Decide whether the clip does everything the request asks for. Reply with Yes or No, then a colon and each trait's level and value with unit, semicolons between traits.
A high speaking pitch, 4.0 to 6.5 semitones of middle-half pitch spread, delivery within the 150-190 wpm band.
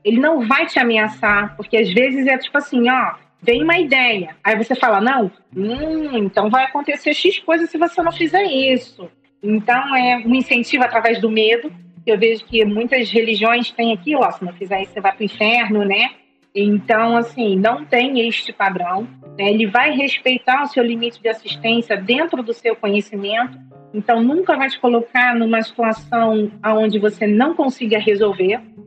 No: high, 230 Hz; average, 3.5 semitones; average, 180 wpm